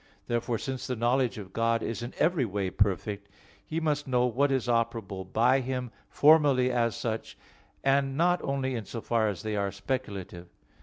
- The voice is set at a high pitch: No, low, 120 Hz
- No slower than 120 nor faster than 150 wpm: No, average, 175 wpm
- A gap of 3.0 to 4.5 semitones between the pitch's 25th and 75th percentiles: Yes, average, 3.7 semitones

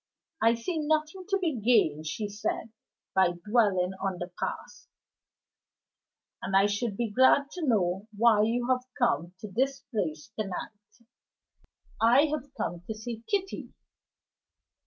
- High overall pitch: Yes, high, 225 Hz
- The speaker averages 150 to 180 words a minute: No, average, 140 wpm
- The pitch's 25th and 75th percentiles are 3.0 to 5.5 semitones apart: Yes, average, 5.0 semitones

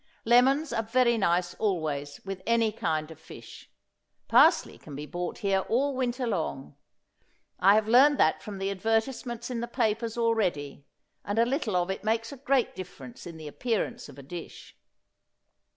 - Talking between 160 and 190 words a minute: Yes, average, 170 wpm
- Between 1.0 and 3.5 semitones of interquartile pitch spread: No, wide, 5.4 semitones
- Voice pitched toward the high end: Yes, high, 215 Hz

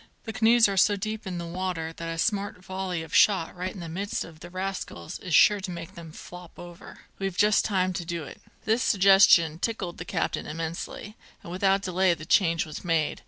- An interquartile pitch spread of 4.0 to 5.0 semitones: No, average, 2.9 semitones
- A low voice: No, medium, 185 Hz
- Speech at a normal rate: No, fast, 210 wpm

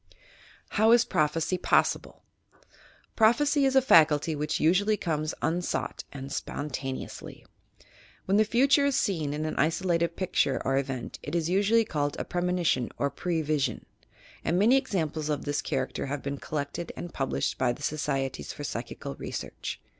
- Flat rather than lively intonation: No, average, 5.2 semitones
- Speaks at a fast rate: No, average, 160 wpm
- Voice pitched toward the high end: No, medium, 160 Hz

